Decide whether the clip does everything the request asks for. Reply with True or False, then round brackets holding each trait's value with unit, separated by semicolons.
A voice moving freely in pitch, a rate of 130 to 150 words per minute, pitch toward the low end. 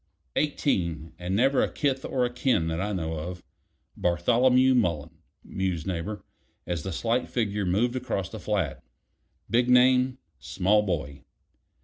True (6.3 semitones; 140 wpm; 105 Hz)